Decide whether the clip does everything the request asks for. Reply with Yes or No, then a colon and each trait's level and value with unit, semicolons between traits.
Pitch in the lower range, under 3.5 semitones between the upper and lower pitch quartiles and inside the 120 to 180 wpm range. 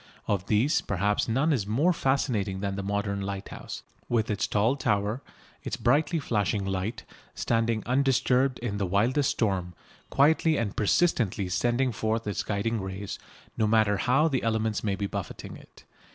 No: low, 110 Hz; average, 4.0 semitones; average, 155 wpm